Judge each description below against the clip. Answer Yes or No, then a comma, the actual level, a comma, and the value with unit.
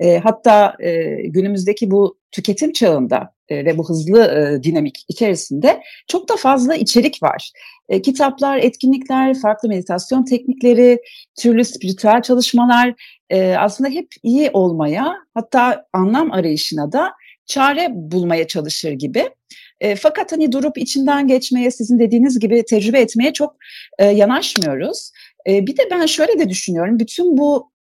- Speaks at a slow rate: No, average, 120 wpm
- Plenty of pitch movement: Yes, wide, 6.1 semitones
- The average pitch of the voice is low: No, high, 240 Hz